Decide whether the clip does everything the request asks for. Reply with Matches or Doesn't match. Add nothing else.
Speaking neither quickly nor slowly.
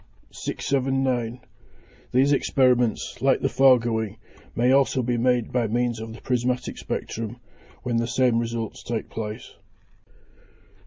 Doesn't match